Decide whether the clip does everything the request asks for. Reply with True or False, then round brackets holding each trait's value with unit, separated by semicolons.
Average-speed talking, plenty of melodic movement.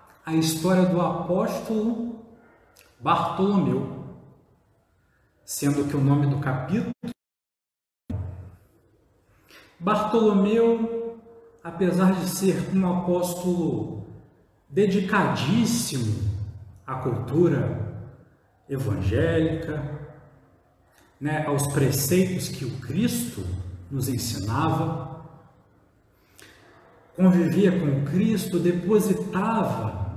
False (70 wpm; 8.3 semitones)